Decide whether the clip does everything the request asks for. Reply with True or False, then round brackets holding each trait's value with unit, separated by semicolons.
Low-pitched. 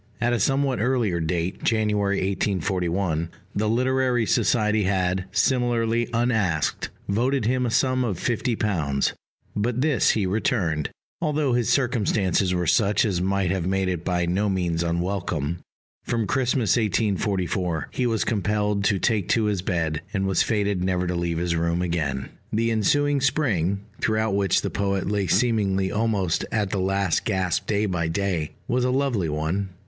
True (100 Hz)